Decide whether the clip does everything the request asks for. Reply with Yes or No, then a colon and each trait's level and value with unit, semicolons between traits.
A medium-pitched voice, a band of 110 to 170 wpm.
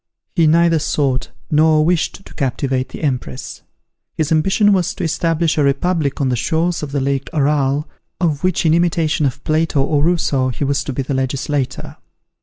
No: medium, 150 Hz; average, 180 wpm